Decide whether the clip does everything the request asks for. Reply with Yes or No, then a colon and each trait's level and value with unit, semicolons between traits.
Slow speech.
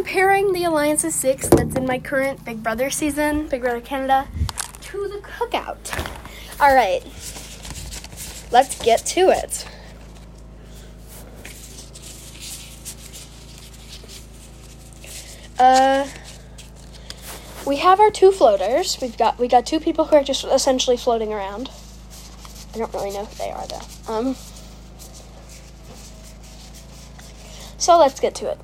Yes: slow, 115 wpm